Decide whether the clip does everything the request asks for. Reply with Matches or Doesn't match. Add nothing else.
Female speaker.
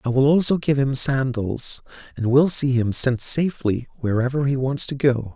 Doesn't match